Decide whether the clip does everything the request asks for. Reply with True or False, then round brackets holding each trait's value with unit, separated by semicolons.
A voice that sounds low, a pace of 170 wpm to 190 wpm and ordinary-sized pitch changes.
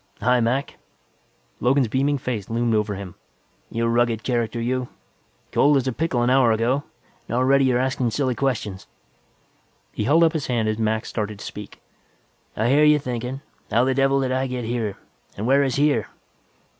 True (125 Hz; 180 wpm; 3.0 semitones)